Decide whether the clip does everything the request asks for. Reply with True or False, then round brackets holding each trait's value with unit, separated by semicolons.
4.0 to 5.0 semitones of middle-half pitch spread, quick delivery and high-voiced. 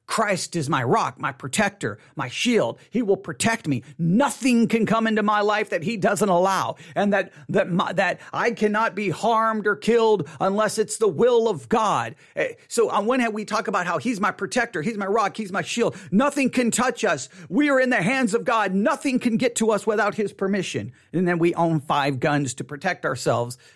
True (4.6 semitones; 210 wpm; 210 Hz)